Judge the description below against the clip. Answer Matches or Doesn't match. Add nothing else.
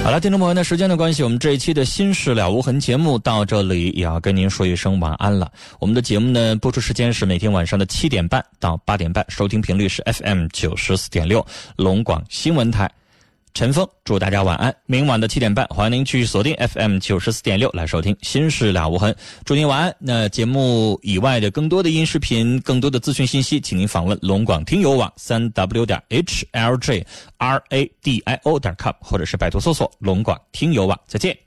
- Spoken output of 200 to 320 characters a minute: Doesn't match